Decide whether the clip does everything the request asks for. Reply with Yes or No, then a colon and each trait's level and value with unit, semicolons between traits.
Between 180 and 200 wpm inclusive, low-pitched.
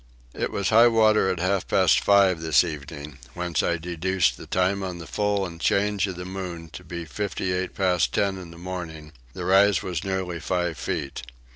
Yes: average, 190 wpm; very low, 90 Hz